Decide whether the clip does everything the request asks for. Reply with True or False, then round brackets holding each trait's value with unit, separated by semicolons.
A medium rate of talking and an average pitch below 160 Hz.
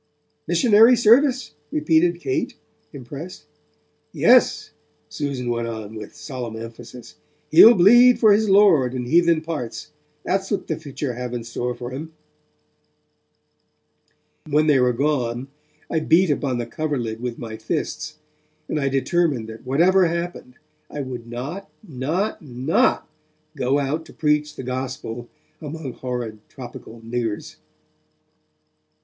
False (130 wpm; 140 Hz)